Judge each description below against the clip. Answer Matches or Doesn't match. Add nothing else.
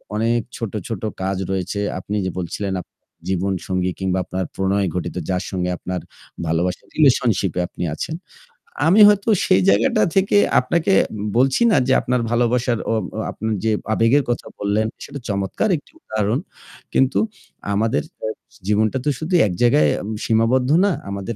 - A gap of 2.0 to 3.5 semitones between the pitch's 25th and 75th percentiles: Doesn't match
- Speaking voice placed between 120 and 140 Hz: Doesn't match